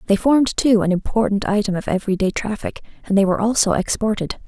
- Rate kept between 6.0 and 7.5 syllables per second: Yes, 6.5 syllables/s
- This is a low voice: No, high, 205 Hz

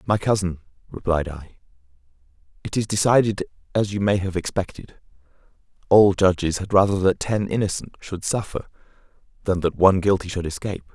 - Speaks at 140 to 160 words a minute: Yes, average, 150 wpm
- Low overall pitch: Yes, very low, 95 Hz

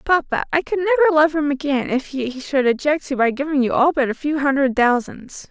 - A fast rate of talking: Yes, fast, 230 wpm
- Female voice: Yes, female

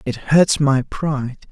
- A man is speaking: Yes, male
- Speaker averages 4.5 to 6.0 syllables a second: No, 3.9 syllables/s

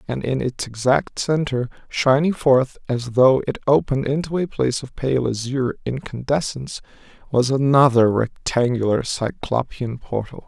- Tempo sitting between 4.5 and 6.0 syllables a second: Yes, 4.7 syllables/s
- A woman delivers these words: No, male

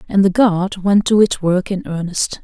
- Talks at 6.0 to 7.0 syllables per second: No, 4.5 syllables/s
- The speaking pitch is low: No, high, 190 Hz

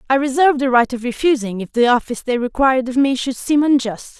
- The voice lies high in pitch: Yes, very high, 255 Hz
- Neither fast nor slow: No, fast, 230 wpm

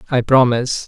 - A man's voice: Yes, male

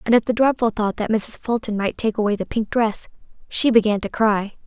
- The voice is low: No, high, 220 Hz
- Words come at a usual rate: No, fast, 230 wpm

